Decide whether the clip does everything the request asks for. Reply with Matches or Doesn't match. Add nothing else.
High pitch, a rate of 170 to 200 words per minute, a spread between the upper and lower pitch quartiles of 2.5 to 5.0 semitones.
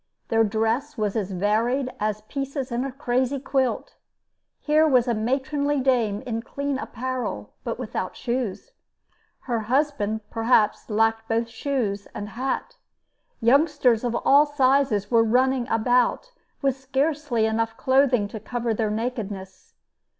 Doesn't match